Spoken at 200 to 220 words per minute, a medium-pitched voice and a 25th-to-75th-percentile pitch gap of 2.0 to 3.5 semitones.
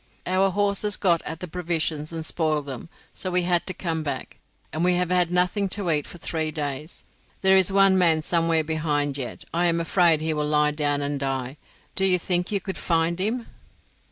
Yes: fast, 205 wpm; medium, 165 Hz; average, 3.0 semitones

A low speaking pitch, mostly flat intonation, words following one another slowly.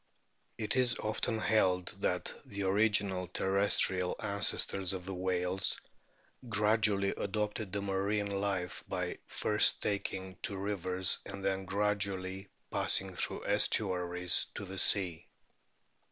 Yes: very low, 95 Hz; narrow, 1.7 semitones; slow, 115 wpm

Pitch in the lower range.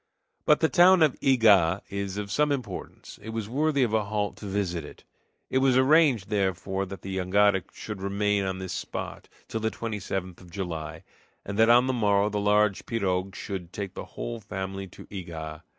Yes: low, 100 Hz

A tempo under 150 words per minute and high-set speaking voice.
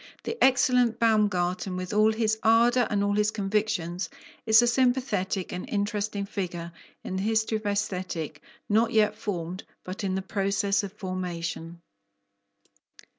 Yes: slow, 135 wpm; high, 205 Hz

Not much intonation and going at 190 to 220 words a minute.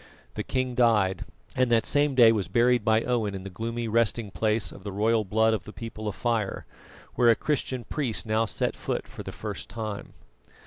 Yes: narrow, 2.1 semitones; average, 200 wpm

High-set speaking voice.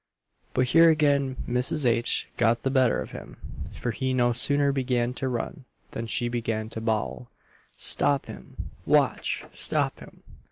No: low, 125 Hz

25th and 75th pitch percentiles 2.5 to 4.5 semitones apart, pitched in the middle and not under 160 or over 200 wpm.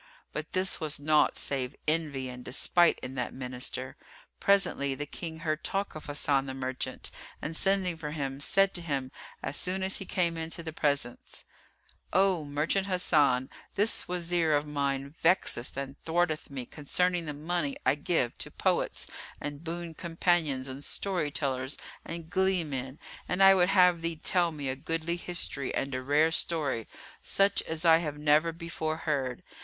Yes: average, 3.9 semitones; medium, 155 Hz; average, 170 wpm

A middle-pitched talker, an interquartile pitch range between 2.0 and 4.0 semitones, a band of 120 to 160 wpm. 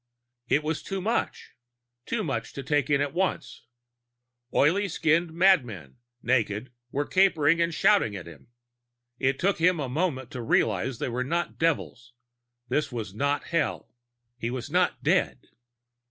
No: medium, 145 Hz; wide, 5.5 semitones; average, 155 wpm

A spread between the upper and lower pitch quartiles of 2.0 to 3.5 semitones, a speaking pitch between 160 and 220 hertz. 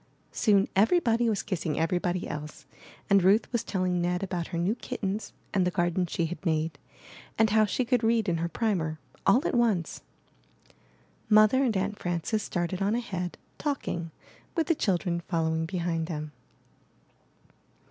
No: average, 4.2 semitones; medium, 185 Hz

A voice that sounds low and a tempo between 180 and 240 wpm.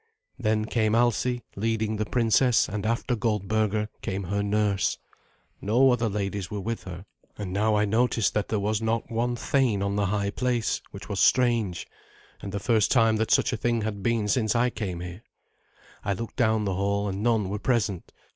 Yes: low, 110 Hz; average, 190 wpm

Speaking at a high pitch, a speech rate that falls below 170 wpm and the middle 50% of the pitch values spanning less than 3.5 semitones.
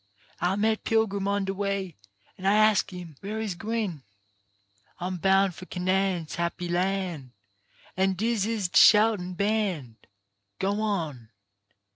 Yes: high, 195 Hz; average, 140 wpm; average, 2.8 semitones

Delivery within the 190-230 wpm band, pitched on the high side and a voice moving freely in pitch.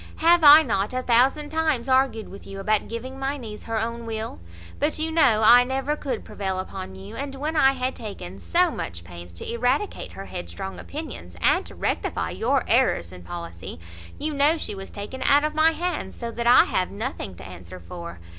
Yes: average, 200 wpm; high, 235 Hz; wide, 6.7 semitones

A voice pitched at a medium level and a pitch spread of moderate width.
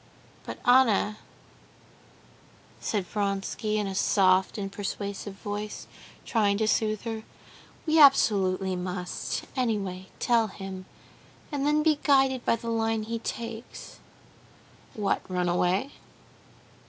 No: high, 210 Hz; average, 3.1 semitones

